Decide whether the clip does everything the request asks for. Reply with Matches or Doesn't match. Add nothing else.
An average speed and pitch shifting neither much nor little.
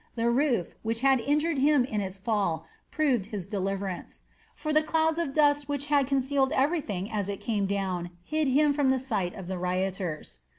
Doesn't match